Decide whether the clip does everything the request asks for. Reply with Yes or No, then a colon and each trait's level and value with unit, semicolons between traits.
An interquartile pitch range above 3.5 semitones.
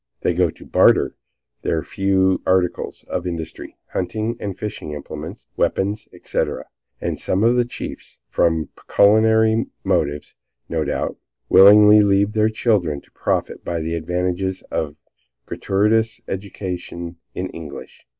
Yes: average, 3.9 semitones